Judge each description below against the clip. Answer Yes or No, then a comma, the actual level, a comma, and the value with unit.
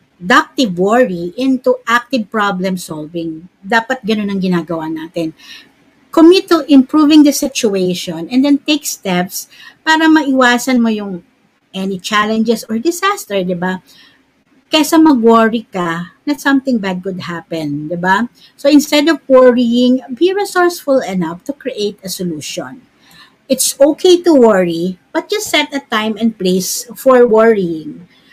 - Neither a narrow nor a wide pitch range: No, wide, 7.1 semitones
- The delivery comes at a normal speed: Yes, average, 135 wpm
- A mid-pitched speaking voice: No, high, 235 Hz